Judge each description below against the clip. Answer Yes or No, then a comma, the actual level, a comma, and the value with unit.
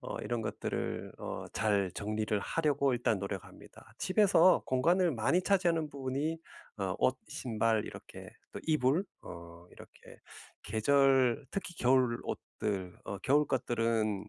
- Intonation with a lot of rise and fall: Yes, wide, 5.8 semitones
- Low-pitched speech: Yes, low, 125 Hz